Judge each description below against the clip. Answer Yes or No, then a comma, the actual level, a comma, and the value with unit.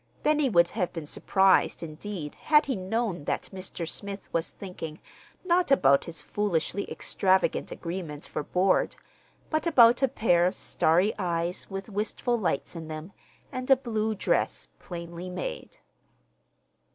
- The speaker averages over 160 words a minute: No, average, 140 wpm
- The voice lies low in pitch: No, high, 190 Hz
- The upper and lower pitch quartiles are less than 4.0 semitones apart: No, average, 4.7 semitones